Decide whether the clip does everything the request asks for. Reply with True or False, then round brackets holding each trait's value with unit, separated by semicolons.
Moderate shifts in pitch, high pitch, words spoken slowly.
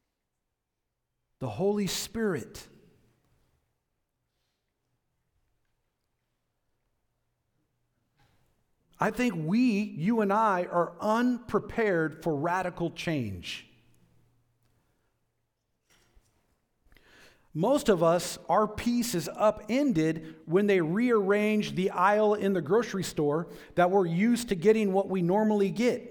True (4.4 semitones; 195 Hz; 90 wpm)